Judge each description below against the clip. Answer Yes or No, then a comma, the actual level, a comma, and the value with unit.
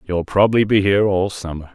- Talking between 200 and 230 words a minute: Yes, fast, 205 wpm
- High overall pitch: No, very low, 95 Hz